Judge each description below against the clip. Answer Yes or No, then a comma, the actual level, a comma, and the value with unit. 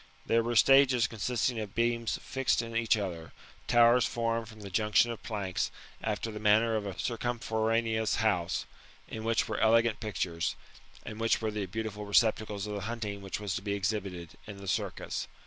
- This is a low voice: Yes, low, 110 Hz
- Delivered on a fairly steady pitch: Yes, narrow, 2.2 semitones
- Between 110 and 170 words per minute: No, average, 180 wpm